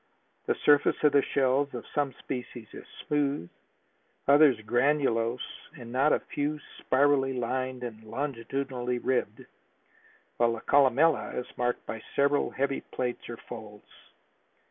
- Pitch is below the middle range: Yes, low, 130 Hz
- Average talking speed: No, slow, 130 wpm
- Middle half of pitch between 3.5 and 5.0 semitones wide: No, average, 2.8 semitones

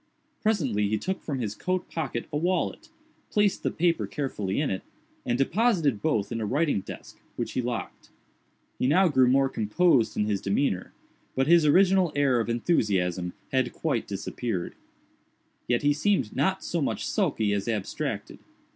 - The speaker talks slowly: No, average, 165 wpm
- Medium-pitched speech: No, low, 130 Hz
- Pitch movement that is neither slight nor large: No, wide, 7.8 semitones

